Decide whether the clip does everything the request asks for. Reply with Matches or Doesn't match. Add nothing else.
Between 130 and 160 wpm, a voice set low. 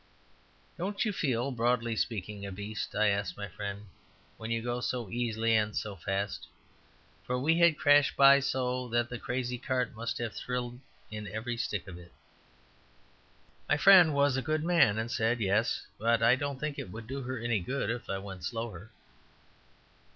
Doesn't match